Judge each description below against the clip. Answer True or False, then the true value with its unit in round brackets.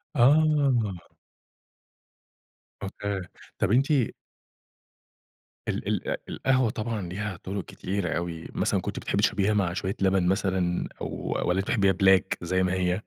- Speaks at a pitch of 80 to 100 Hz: True (95 Hz)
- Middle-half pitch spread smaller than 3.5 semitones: True (2.8 semitones)